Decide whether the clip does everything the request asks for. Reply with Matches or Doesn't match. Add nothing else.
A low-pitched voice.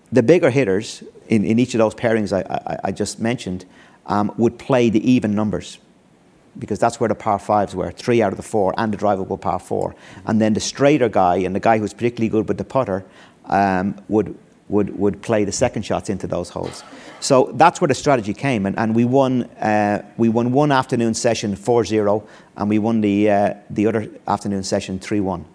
Matches